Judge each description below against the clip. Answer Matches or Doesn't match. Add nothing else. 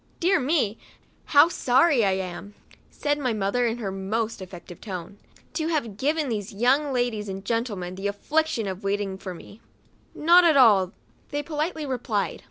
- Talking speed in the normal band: Matches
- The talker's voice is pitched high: Matches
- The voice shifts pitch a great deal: Matches